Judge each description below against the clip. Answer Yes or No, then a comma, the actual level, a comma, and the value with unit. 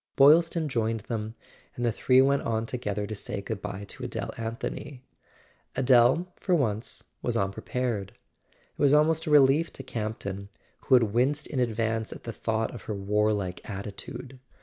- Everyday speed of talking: Yes, average, 170 wpm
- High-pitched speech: No, low, 115 Hz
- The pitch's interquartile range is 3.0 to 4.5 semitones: Yes, average, 4.2 semitones